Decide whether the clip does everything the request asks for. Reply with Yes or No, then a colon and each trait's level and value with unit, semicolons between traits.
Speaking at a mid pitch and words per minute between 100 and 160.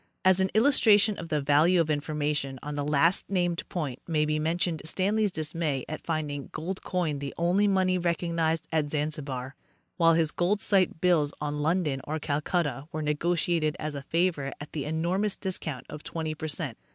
No: medium, 160 Hz; average, 185 wpm